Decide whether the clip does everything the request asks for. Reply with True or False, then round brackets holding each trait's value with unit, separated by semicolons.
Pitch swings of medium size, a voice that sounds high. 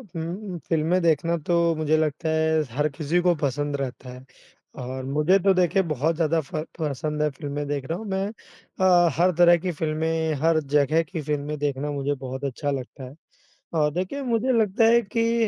False (3.4 semitones; 155 Hz)